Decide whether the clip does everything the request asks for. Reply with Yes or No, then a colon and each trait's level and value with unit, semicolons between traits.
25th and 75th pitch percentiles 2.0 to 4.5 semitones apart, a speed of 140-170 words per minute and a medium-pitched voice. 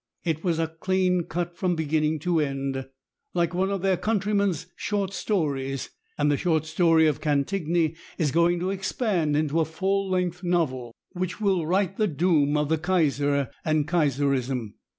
Yes: average, 3.9 semitones; average, 160 wpm; medium, 165 Hz